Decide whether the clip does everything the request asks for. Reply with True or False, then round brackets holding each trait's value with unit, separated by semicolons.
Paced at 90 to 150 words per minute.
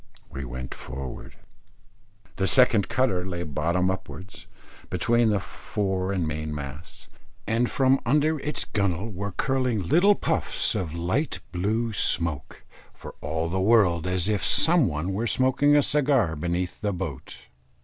True (145 wpm)